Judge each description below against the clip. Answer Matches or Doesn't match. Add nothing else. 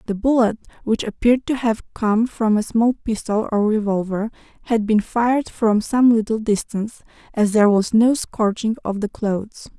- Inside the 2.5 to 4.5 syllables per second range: Doesn't match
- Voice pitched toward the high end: Matches